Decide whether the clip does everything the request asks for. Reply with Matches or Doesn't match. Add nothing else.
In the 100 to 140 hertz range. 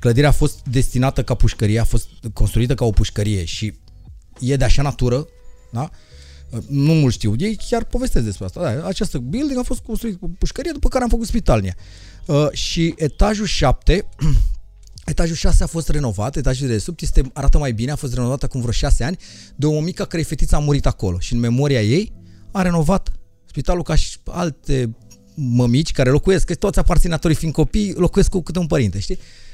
Matches